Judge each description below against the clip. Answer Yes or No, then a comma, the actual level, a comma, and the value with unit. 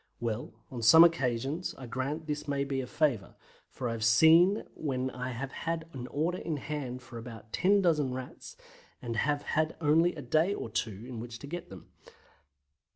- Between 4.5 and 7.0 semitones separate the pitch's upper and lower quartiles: Yes, average, 4.9 semitones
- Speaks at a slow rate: No, average, 190 wpm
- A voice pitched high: No, low, 135 Hz